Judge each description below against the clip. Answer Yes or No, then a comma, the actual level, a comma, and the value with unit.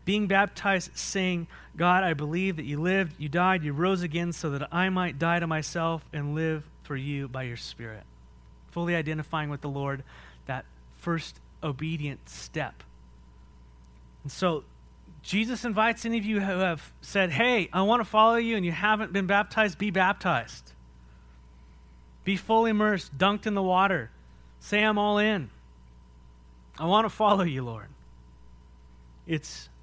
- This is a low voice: No, medium, 160 Hz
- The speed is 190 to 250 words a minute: No, average, 155 wpm